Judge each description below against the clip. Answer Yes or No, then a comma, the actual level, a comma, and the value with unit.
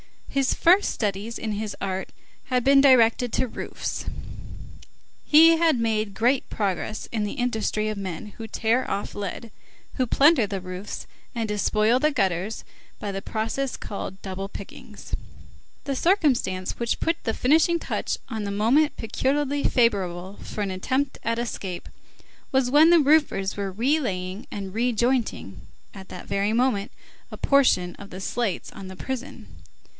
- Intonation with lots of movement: No, average, 5.0 semitones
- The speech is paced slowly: No, average, 160 wpm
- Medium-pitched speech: No, high, 225 Hz